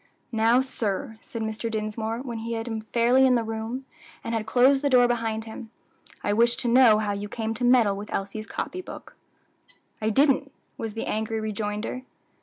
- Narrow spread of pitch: Yes, narrow, 2.1 semitones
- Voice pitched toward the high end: Yes, high, 225 Hz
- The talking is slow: No, average, 190 wpm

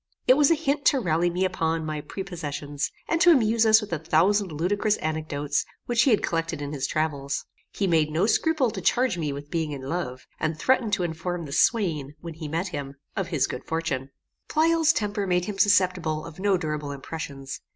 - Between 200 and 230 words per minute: Yes, fast, 205 wpm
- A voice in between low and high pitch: Yes, medium, 165 Hz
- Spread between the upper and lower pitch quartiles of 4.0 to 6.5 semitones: Yes, average, 5.2 semitones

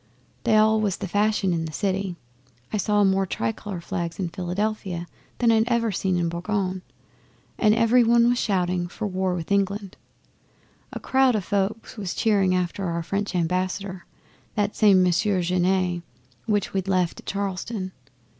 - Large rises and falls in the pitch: No, average, 2.7 semitones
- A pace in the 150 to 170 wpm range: Yes, average, 160 wpm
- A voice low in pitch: No, high, 195 Hz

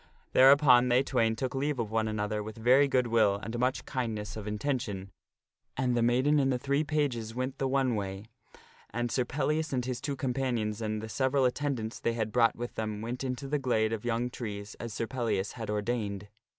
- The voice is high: No, low, 120 Hz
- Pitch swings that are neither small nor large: Yes, average, 3.2 semitones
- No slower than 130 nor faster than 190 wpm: No, fast, 205 wpm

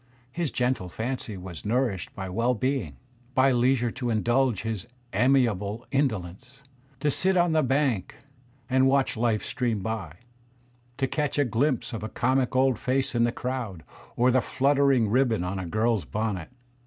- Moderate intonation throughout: Yes, average, 3.8 semitones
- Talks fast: No, average, 160 wpm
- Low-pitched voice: Yes, low, 120 Hz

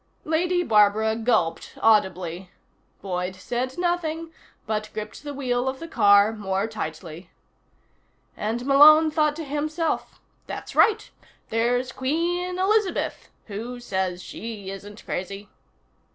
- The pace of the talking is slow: Yes, slow, 115 wpm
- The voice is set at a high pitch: Yes, high, 230 Hz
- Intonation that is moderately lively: No, wide, 7.3 semitones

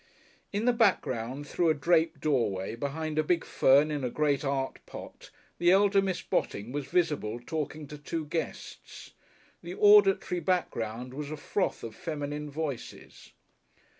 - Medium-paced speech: Yes, average, 150 wpm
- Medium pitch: Yes, medium, 150 Hz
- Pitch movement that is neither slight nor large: Yes, average, 4.2 semitones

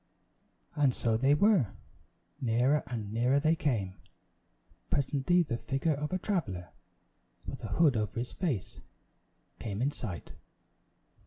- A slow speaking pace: Yes, slow, 130 wpm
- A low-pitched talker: Yes, low, 130 Hz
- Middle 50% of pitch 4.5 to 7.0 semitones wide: Yes, average, 5.0 semitones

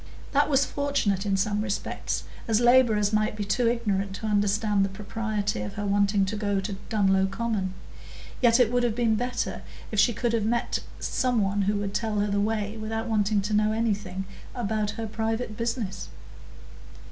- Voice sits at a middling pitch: No, high, 215 Hz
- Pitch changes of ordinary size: No, narrow, 2.2 semitones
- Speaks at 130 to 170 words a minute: No, average, 180 wpm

